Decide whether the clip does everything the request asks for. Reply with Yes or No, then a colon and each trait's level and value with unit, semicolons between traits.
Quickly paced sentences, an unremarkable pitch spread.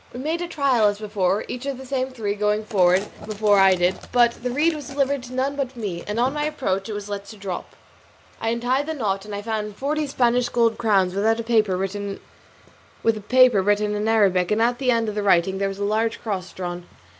Yes: fast, 215 wpm; average, 3.9 semitones